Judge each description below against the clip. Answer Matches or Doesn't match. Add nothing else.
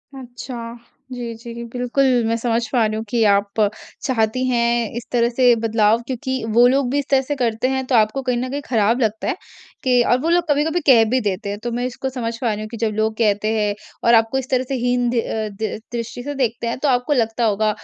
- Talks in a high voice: Matches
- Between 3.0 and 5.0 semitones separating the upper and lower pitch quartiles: Doesn't match